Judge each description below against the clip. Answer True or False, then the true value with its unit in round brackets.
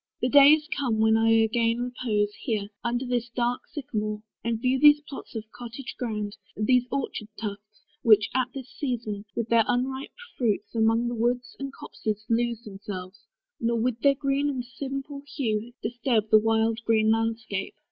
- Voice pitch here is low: False (235 Hz)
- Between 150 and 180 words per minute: True (165 wpm)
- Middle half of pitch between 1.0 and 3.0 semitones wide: True (2.6 semitones)